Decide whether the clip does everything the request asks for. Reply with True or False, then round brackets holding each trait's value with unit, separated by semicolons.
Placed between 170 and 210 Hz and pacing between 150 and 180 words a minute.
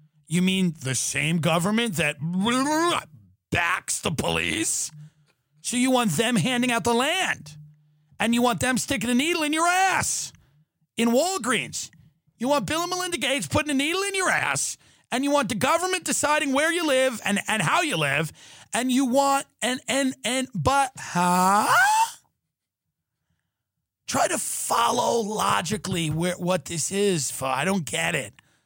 False (225 Hz; 160 wpm)